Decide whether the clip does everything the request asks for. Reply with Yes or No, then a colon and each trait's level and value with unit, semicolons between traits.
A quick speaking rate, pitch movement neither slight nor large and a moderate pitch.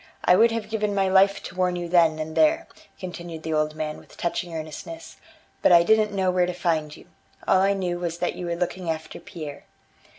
Yes: fast, 220 wpm; average, 3.2 semitones; medium, 180 Hz